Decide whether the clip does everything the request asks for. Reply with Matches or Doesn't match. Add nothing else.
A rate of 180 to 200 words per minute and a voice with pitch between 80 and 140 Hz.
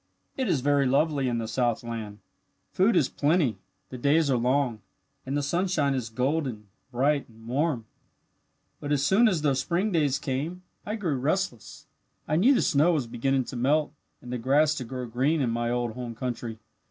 Matches